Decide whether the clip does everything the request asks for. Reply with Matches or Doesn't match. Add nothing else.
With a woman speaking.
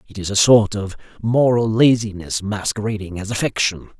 Doesn't match